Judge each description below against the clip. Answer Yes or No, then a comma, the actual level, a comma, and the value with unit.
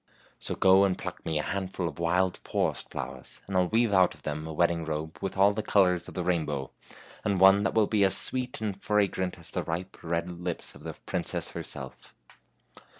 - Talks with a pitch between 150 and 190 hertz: No, very low, 90 Hz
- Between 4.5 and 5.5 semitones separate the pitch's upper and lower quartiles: No, average, 2.9 semitones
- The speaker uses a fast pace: Yes, fast, 220 wpm